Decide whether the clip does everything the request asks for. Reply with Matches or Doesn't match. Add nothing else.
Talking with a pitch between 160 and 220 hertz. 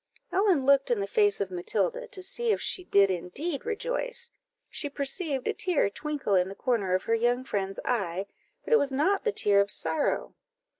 Doesn't match